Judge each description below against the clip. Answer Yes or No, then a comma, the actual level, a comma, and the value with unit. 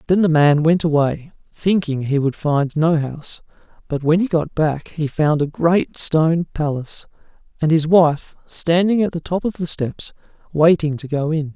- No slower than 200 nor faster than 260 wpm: No, average, 185 wpm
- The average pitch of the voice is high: No, medium, 160 Hz